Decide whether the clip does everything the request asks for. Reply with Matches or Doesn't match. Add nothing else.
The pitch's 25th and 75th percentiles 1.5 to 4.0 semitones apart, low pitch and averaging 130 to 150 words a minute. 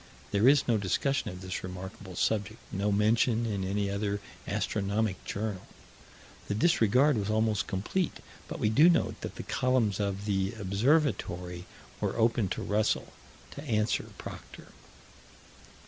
Matches